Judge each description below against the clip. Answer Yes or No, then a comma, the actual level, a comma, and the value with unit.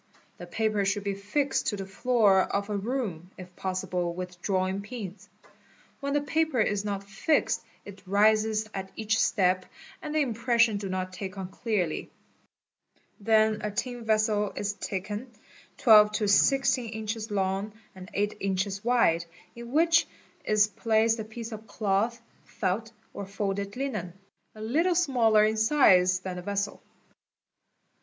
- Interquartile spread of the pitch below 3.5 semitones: Yes, average, 3.0 semitones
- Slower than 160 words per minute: Yes, average, 150 wpm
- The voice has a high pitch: Yes, high, 210 Hz